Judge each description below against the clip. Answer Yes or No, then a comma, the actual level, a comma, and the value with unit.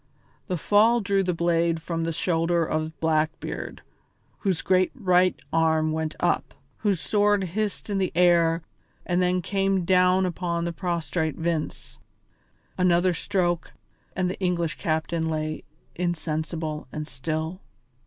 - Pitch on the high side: No, medium, 170 Hz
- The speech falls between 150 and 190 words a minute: No, slow, 135 wpm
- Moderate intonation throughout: No, narrow, 2.3 semitones